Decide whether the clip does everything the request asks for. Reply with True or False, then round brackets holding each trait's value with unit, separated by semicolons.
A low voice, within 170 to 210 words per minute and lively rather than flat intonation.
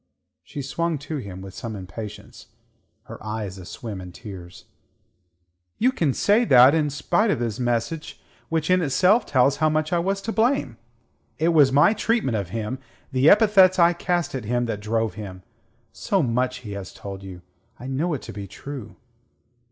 True (130 Hz; 180 wpm; 7.9 semitones)